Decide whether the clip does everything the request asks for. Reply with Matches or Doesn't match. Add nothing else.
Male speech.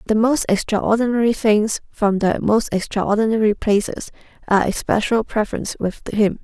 Doesn't match